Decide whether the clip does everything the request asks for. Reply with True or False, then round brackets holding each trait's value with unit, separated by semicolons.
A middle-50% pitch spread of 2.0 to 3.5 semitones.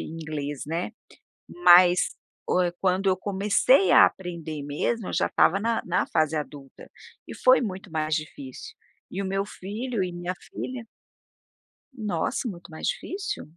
False (4.3 semitones)